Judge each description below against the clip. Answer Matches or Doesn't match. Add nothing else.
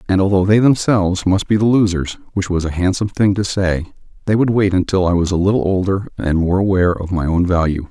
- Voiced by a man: Matches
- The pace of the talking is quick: Matches